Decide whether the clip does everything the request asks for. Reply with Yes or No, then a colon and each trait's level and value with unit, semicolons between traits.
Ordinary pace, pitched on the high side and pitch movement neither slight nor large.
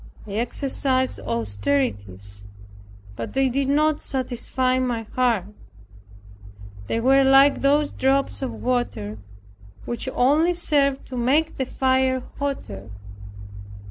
No: slow, 110 wpm; very high, 255 Hz; average, 4.7 semitones